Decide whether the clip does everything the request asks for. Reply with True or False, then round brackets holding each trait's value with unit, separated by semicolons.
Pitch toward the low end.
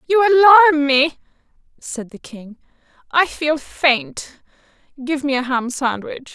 False (285 Hz)